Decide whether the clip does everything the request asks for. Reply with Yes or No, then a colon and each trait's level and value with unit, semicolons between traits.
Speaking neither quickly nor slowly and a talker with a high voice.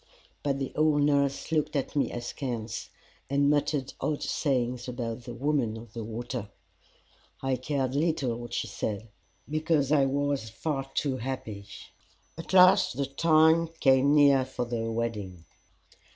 No: average, 145 wpm; low, 135 Hz